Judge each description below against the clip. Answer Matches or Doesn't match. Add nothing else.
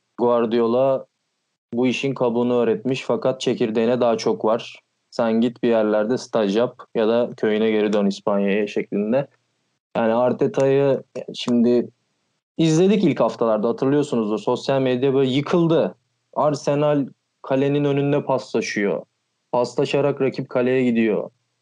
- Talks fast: Doesn't match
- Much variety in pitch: Doesn't match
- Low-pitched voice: Matches